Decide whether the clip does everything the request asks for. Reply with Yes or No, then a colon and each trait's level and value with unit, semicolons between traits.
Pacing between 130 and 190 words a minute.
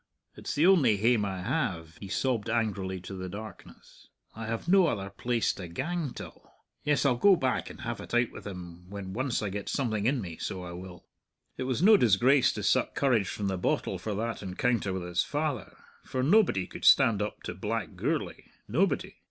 No: average, 200 wpm